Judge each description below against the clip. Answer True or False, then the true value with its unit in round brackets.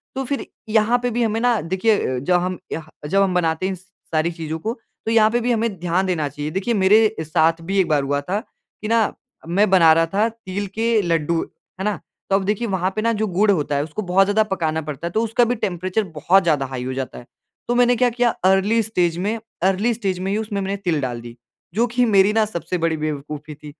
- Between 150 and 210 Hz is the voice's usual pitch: True (190 Hz)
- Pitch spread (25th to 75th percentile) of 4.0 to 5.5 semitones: True (5.0 semitones)